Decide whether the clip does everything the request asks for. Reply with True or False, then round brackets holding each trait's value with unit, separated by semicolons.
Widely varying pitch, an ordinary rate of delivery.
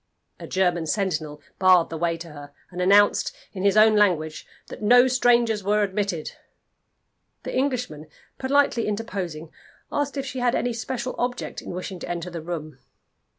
True (6.0 semitones; 160 wpm)